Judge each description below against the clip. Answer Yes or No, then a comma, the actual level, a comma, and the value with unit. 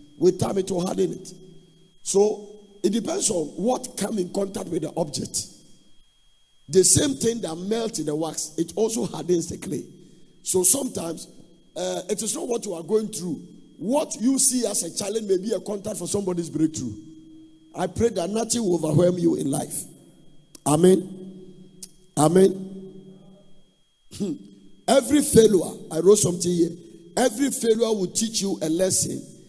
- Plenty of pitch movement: No, average, 3.7 semitones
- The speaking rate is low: No, average, 160 wpm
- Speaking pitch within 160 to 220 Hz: Yes, medium, 185 Hz